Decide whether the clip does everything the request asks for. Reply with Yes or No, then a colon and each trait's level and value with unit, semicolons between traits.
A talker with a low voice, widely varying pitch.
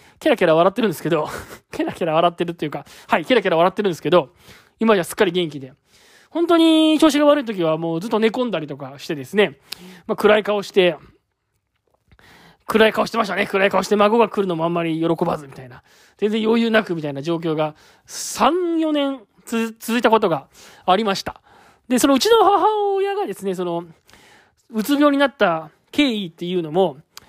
No: high, 200 Hz; wide, 5.8 semitones